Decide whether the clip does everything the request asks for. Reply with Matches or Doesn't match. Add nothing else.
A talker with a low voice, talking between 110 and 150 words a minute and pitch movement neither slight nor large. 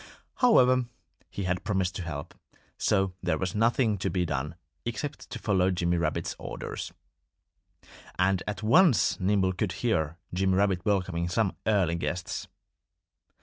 Matches